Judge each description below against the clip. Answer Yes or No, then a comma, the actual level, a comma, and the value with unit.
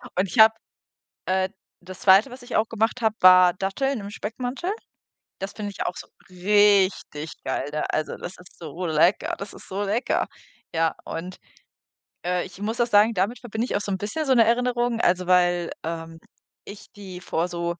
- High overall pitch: Yes, high, 195 Hz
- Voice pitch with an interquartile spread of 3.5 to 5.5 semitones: Yes, average, 3.8 semitones